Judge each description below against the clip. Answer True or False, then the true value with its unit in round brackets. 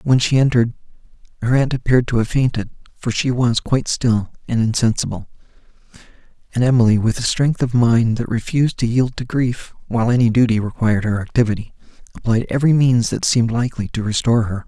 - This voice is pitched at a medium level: False (120 Hz)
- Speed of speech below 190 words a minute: True (180 wpm)